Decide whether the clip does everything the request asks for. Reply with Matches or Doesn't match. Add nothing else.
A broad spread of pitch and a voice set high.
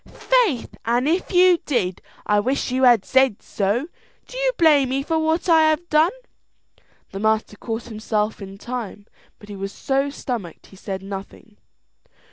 Matches